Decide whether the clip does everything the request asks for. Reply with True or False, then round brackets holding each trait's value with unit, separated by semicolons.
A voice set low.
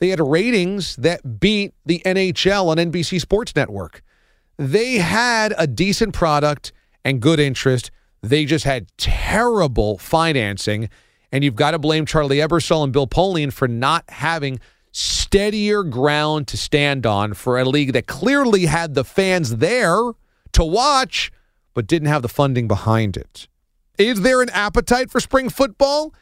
False (160 Hz)